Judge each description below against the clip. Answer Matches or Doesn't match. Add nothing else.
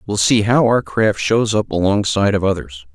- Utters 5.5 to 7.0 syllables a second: Doesn't match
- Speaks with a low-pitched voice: Matches